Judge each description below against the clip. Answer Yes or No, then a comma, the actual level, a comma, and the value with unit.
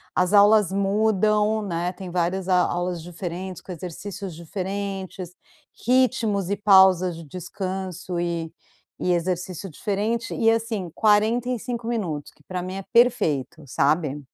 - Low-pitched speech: No, high, 190 Hz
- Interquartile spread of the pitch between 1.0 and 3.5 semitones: Yes, average, 3.2 semitones